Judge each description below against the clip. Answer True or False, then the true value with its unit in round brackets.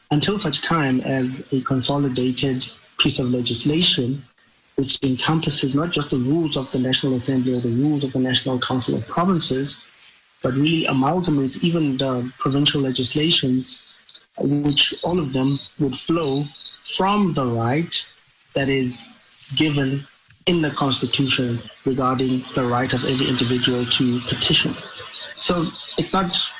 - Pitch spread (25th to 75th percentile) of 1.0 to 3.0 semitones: True (2.7 semitones)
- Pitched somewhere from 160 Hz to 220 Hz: False (135 Hz)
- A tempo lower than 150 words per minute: True (140 wpm)